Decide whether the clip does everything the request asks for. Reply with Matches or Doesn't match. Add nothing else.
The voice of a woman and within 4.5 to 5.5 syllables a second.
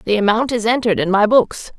Doesn't match